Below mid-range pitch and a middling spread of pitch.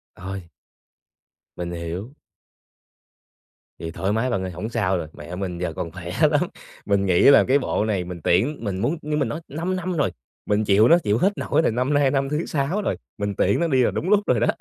No: low, 110 Hz; wide, 7.7 semitones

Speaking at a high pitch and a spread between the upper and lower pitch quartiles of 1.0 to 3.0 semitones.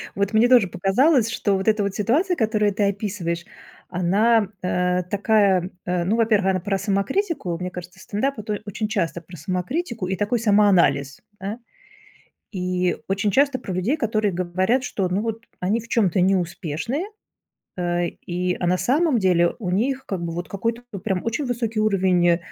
No: high, 200 Hz; average, 3.9 semitones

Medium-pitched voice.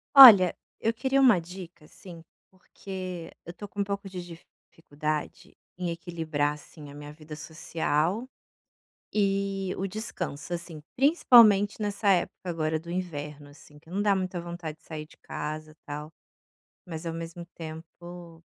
Yes: medium, 170 Hz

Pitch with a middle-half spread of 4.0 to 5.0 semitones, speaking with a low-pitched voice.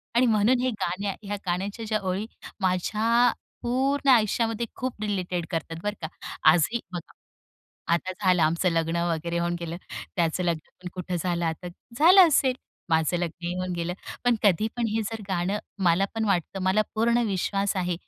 No: average, 4.3 semitones; medium, 185 Hz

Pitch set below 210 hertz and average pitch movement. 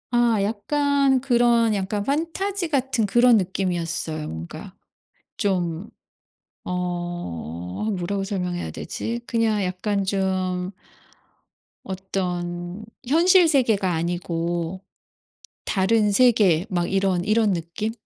Yes: high, 195 Hz; average, 4.8 semitones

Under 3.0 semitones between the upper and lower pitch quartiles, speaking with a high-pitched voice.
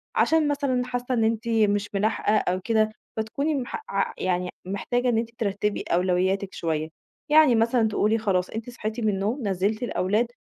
No: average, 3.7 semitones; high, 220 Hz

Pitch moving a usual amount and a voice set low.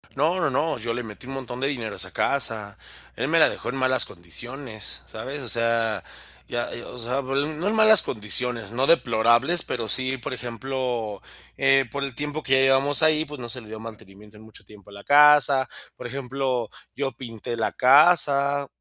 Yes: average, 3.5 semitones; low, 130 Hz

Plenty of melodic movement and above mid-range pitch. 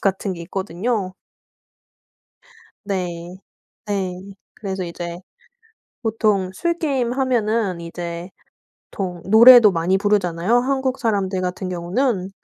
No: average, 4.2 semitones; high, 195 Hz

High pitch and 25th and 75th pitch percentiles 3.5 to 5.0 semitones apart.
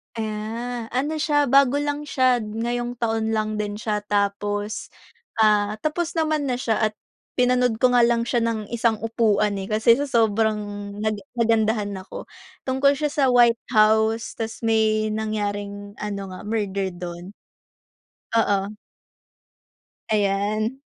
No: high, 220 Hz; average, 2.7 semitones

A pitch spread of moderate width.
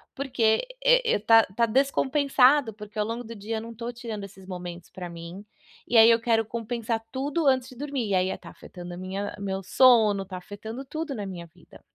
Yes: average, 4.6 semitones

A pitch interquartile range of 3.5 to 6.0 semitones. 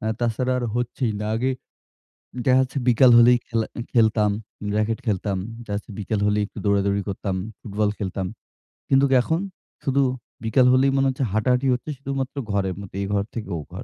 Yes: average, 4.1 semitones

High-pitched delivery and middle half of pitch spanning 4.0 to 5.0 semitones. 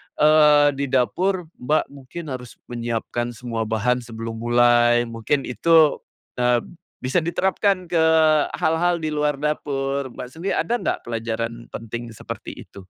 No: low, 130 Hz; average, 4.7 semitones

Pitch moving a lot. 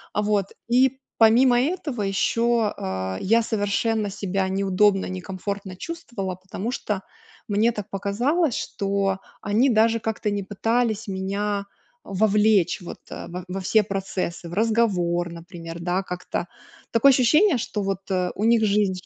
No: average, 3.2 semitones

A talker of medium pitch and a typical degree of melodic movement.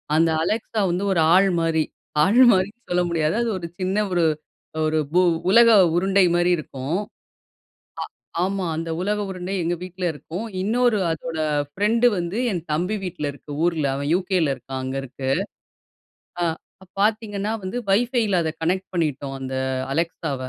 Yes: medium, 180 Hz; average, 3.9 semitones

